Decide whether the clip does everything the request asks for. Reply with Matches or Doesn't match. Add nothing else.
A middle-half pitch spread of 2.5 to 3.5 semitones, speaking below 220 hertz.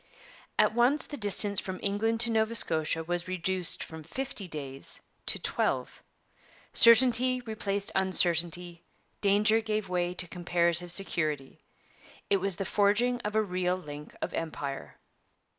Doesn't match